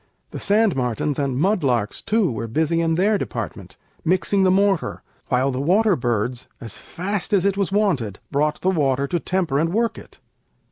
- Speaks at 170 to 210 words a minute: Yes, average, 185 wpm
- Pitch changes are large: Yes, wide, 6.8 semitones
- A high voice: No, medium, 165 Hz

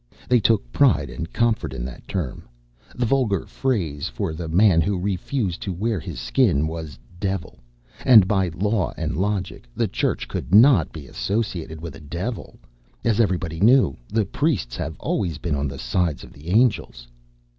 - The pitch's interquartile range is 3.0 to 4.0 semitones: No, wide, 5.6 semitones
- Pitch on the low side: Yes, very low, 90 Hz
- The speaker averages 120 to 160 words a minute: No, average, 170 wpm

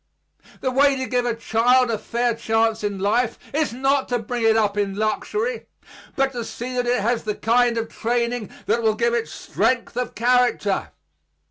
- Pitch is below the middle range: No, high, 235 Hz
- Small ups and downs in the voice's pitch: Yes, narrow, 2.1 semitones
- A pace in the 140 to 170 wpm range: No, average, 190 wpm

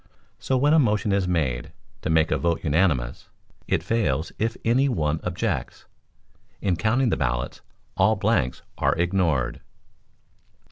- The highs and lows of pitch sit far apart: Yes, wide, 6.4 semitones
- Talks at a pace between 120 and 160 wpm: Yes, average, 140 wpm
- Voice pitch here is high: No, very low, 90 Hz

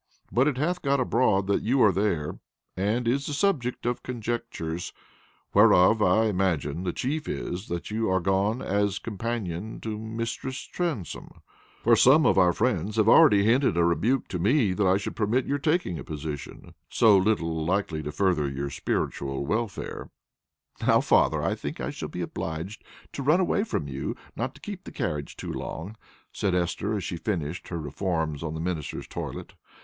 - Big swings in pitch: Yes, wide, 5.7 semitones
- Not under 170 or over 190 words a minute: Yes, average, 180 wpm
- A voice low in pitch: Yes, low, 100 Hz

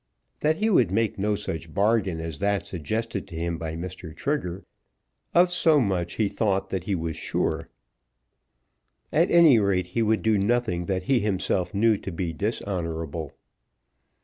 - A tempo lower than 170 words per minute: Yes, average, 160 wpm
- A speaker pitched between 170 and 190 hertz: No, low, 100 Hz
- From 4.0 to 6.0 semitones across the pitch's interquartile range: Yes, average, 4.7 semitones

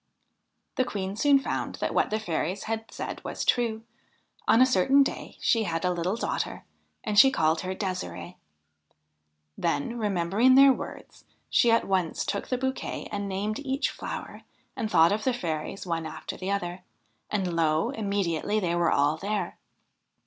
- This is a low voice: No, high, 200 Hz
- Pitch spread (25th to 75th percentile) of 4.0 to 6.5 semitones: Yes, average, 4.9 semitones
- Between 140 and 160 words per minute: No, average, 170 wpm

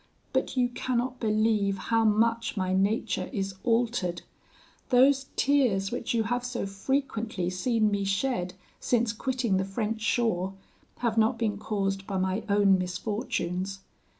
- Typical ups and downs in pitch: Yes, average, 3.5 semitones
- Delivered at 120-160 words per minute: Yes, average, 140 wpm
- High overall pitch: Yes, high, 215 Hz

